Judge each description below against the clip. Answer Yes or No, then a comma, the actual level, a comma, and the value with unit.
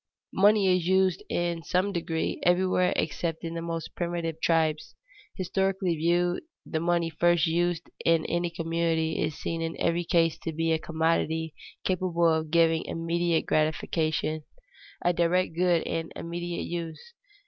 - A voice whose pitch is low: No, medium, 170 Hz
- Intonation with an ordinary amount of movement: No, narrow, 1.2 semitones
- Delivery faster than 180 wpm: No, average, 145 wpm